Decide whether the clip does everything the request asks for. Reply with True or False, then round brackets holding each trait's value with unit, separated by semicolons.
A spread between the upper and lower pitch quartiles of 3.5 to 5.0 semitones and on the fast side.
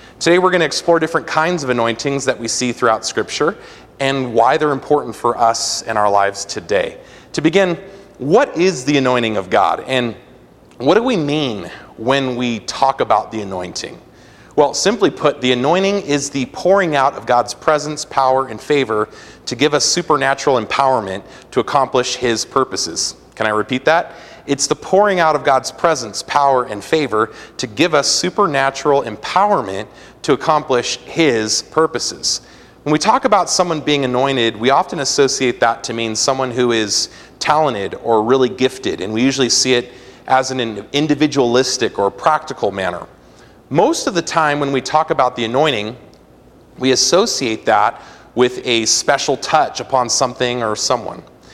False (4.6 semitones; 165 wpm)